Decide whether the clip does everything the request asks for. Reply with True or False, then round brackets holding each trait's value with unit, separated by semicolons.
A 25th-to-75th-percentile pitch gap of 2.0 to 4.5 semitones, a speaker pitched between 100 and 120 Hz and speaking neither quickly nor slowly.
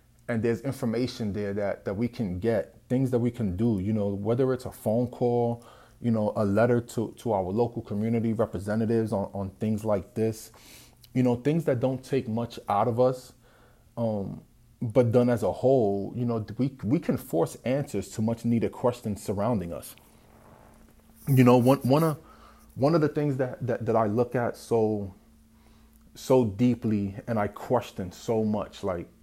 True (2.5 semitones; 115 Hz; 185 wpm)